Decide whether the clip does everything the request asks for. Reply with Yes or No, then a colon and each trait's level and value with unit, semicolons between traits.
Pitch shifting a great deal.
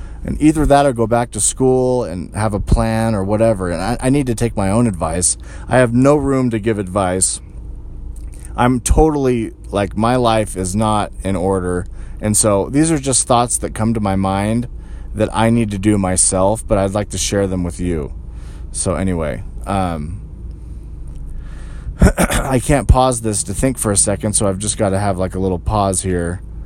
No: average, 4.3 semitones